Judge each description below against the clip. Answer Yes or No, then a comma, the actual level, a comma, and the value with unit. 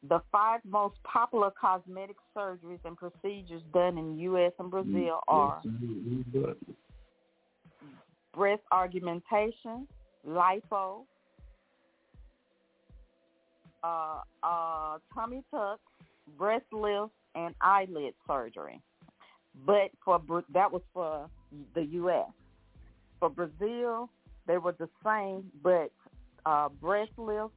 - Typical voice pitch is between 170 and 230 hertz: Yes, medium, 185 Hz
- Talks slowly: Yes, slow, 95 wpm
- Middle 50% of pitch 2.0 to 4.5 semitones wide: Yes, average, 3.7 semitones